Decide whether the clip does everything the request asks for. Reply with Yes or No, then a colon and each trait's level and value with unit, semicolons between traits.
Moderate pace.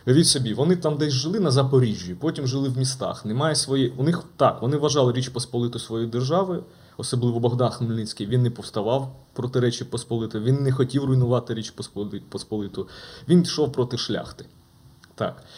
No: fast, 165 wpm